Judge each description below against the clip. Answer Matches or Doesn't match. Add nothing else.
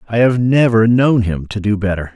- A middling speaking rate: Doesn't match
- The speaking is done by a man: Matches